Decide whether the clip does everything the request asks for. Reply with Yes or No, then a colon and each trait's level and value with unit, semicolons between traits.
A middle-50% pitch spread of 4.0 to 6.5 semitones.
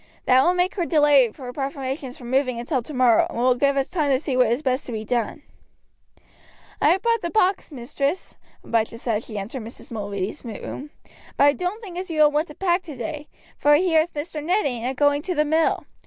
Yes: average, 4.5 semitones